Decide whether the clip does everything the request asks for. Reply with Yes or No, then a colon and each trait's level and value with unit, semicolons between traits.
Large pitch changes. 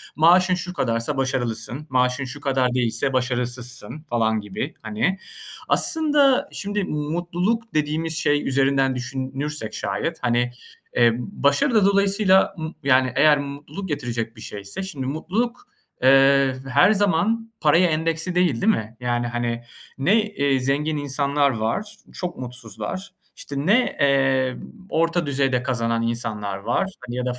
Yes: wide, 5.9 semitones